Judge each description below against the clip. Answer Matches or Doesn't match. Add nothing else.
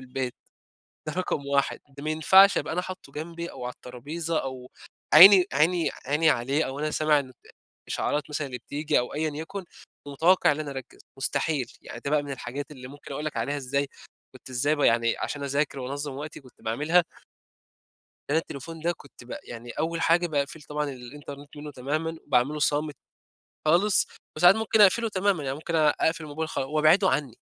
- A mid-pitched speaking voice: Matches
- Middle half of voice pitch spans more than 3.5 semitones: Doesn't match